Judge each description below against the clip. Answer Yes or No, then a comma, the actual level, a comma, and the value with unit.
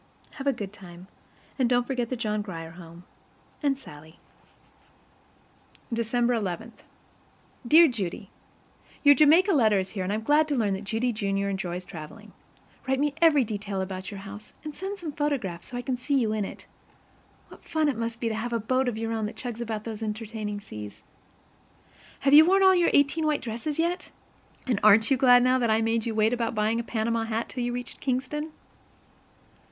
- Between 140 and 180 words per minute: No, average, 195 wpm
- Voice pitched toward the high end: Yes, high, 230 Hz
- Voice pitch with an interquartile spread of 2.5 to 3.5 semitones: No, average, 4.4 semitones